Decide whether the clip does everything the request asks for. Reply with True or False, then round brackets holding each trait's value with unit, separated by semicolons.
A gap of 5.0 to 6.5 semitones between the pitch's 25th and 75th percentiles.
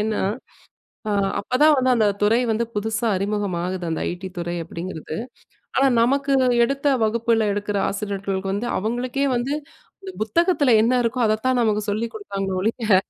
False (3.7 semitones)